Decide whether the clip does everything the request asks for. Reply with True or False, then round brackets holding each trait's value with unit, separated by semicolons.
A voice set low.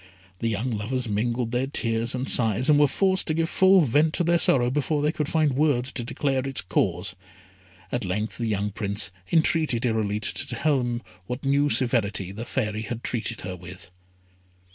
True (120 Hz)